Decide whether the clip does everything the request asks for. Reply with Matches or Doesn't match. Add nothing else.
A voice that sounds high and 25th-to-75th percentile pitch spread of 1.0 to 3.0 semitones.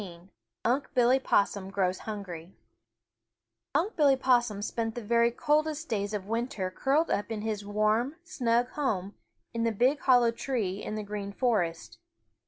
Doesn't match